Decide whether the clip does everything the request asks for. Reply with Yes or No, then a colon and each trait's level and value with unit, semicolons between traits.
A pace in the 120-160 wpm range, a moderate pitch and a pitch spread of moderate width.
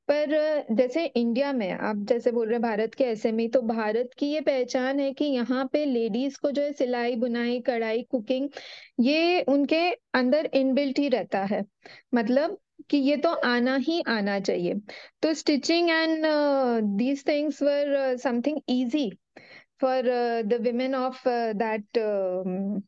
No: average, 150 wpm; very high, 260 Hz; average, 3.4 semitones